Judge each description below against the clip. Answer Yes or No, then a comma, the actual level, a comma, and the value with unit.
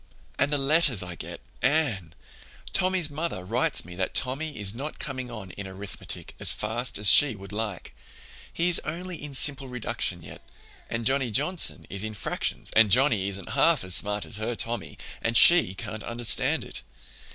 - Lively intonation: Yes, wide, 6.2 semitones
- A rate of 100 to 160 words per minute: No, average, 175 wpm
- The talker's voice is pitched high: No, low, 115 Hz